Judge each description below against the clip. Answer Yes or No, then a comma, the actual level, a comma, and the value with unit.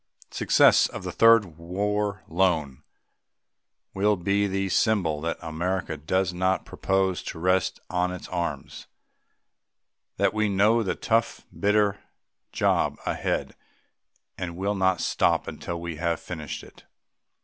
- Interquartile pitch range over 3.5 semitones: No, average, 3.1 semitones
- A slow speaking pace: Yes, slow, 125 wpm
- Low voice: Yes, very low, 95 Hz